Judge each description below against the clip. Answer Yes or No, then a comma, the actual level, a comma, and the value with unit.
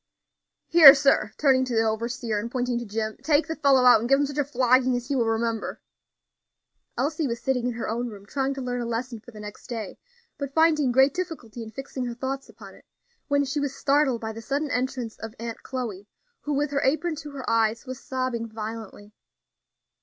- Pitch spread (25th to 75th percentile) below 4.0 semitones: Yes, average, 3.4 semitones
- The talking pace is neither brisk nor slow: No, fast, 215 wpm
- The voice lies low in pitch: No, very high, 250 Hz